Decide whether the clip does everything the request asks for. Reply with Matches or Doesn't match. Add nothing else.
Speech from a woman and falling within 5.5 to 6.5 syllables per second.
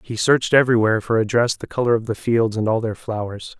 Doesn't match